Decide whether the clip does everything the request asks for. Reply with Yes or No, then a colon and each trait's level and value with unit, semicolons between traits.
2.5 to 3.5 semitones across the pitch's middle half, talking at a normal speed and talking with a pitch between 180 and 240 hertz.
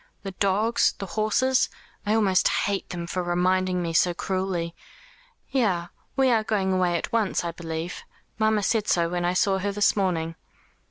Yes: average, 3.2 semitones; average, 170 wpm; high, 190 Hz